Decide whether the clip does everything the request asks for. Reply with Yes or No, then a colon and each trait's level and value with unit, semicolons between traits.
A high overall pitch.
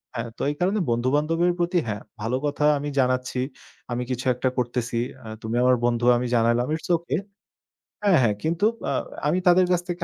No: low, 130 Hz